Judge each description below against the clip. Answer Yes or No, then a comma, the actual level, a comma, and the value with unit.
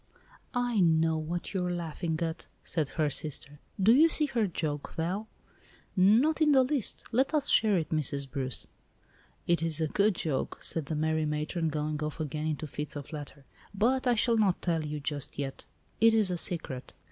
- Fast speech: No, average, 190 wpm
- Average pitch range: No, wide, 5.9 semitones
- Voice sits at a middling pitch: Yes, medium, 165 Hz